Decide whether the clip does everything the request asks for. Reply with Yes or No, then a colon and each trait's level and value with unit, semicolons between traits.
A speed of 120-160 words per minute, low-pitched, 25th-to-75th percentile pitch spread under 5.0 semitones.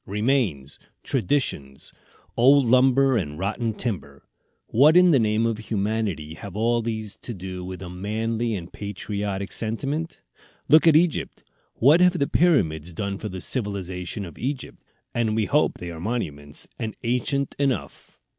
No: average, 150 wpm; low, 110 Hz; wide, 5.5 semitones